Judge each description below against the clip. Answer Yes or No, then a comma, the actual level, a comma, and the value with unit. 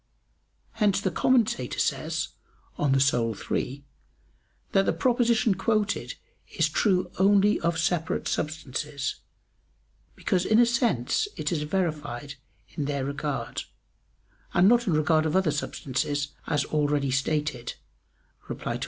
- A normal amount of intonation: No, wide, 5.7 semitones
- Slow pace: Yes, slow, 125 wpm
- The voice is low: No, medium, 155 Hz